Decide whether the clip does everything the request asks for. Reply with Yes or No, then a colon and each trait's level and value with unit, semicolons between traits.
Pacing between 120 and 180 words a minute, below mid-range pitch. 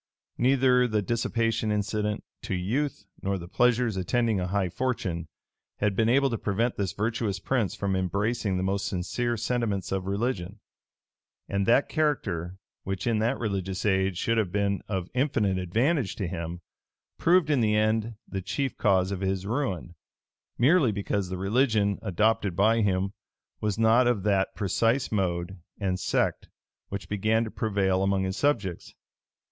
Yes: average, 155 wpm; low, 105 Hz